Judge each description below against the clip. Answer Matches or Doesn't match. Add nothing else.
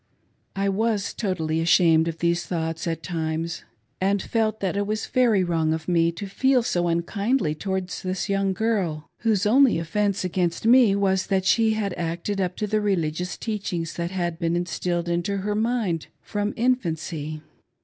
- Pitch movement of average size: Matches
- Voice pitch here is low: Doesn't match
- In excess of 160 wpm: Matches